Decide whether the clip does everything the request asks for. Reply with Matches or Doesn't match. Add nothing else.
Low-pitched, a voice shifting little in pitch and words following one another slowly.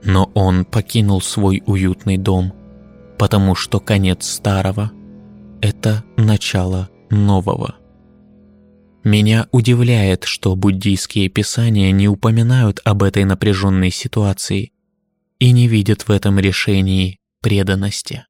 Matches